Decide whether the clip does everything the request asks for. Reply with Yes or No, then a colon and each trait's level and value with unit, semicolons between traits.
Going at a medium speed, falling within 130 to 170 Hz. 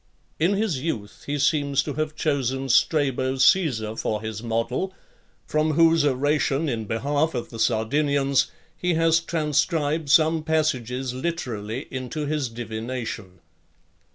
No: slow, 125 wpm; medium, 140 Hz